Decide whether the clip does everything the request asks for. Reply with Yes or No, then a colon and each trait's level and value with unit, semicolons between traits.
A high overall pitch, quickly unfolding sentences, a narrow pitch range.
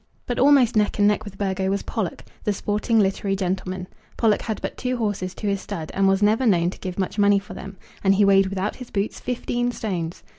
Yes: high, 200 Hz; fast, 225 wpm; narrow, 2.2 semitones